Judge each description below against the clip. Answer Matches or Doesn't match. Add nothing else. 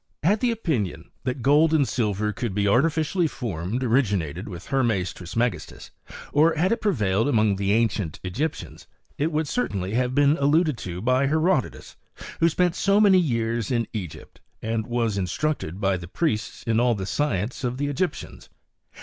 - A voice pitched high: Doesn't match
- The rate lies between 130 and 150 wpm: Doesn't match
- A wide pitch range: Matches